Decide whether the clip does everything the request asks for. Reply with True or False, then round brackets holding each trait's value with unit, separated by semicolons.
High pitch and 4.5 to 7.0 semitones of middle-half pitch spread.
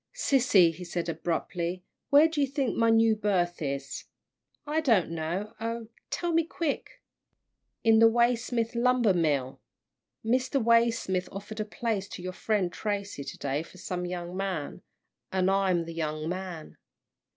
True (195 Hz; 5.0 semitones)